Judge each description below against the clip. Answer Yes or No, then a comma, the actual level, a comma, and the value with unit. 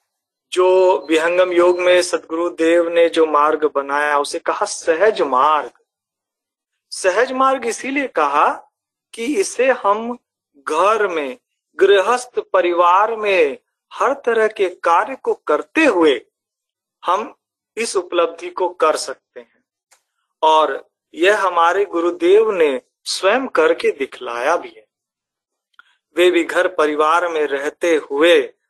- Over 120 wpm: No, average, 115 wpm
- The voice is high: Yes, high, 205 Hz